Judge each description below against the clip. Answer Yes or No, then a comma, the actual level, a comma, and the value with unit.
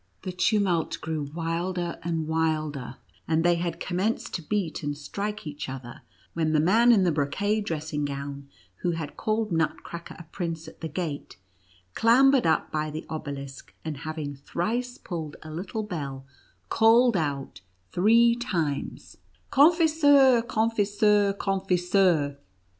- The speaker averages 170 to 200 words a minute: No, average, 140 wpm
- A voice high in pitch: No, medium, 170 Hz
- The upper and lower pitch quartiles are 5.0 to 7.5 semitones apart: Yes, wide, 5.4 semitones